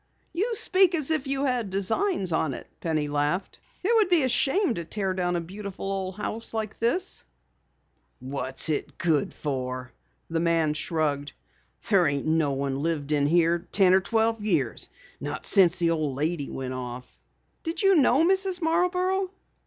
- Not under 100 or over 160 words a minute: No, average, 170 wpm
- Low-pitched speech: No, medium, 185 Hz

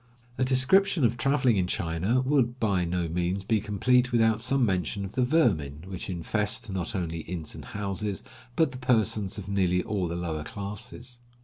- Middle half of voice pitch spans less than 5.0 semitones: No, wide, 5.5 semitones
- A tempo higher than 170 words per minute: Yes, average, 180 wpm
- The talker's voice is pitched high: No, low, 100 Hz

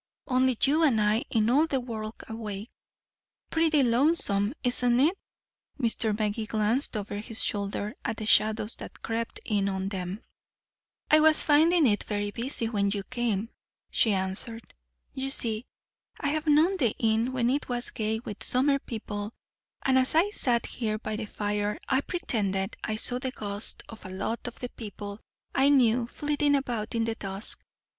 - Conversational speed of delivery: Yes, average, 170 wpm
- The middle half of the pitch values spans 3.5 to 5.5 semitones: Yes, average, 4.0 semitones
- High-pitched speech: Yes, high, 230 Hz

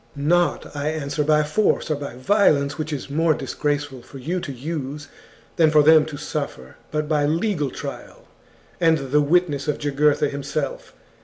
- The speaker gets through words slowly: No, average, 185 wpm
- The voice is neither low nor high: Yes, medium, 150 Hz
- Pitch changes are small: Yes, narrow, 2.0 semitones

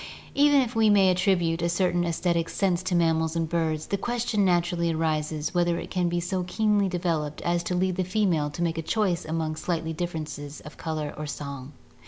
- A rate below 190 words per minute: No, average, 200 wpm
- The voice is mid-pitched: Yes, medium, 170 Hz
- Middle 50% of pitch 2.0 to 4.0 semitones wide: Yes, narrow, 2.6 semitones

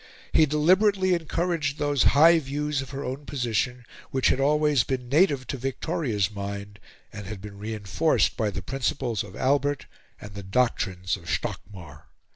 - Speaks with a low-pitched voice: Yes, low, 130 Hz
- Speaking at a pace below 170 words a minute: Yes, average, 155 wpm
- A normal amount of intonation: No, wide, 6.3 semitones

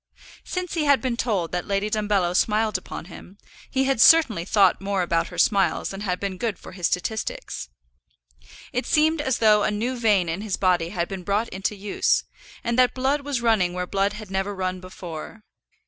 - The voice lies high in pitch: Yes, high, 205 Hz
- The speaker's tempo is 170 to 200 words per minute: Yes, average, 195 wpm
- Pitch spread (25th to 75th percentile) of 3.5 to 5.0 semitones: Yes, average, 4.1 semitones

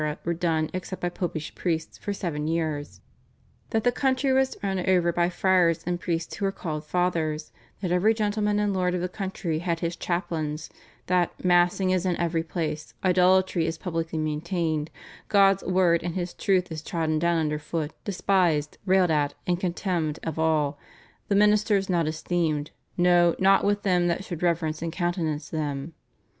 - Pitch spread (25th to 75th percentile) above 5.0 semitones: No, average, 2.7 semitones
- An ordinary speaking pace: Yes, average, 170 wpm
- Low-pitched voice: No, medium, 175 Hz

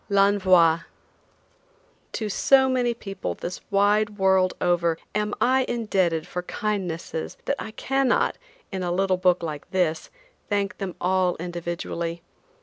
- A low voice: No, high, 190 Hz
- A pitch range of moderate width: Yes, average, 3.2 semitones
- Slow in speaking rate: Yes, slow, 130 wpm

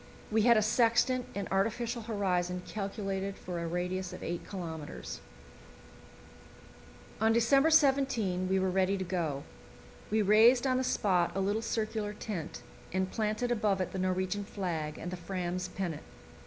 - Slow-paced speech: No, average, 155 wpm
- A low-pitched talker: No, high, 195 Hz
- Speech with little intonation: No, average, 3.5 semitones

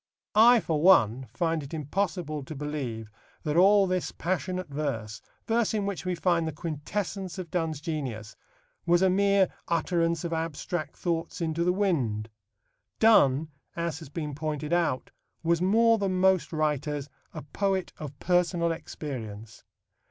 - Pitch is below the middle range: No, medium, 165 Hz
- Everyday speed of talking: Yes, average, 145 wpm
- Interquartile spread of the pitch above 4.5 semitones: No, average, 3.9 semitones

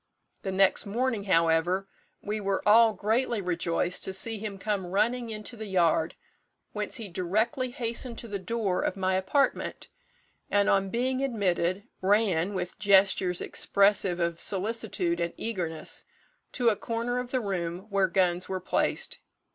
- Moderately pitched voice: No, high, 200 Hz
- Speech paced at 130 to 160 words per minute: Yes, average, 150 wpm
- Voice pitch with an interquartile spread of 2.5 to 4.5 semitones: Yes, average, 3.8 semitones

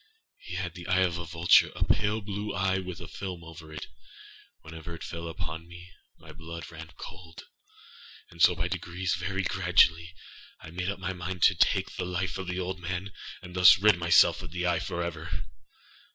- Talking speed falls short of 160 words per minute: No, average, 180 wpm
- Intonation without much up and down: Yes, narrow, 2.0 semitones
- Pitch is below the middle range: Yes, very low, 90 Hz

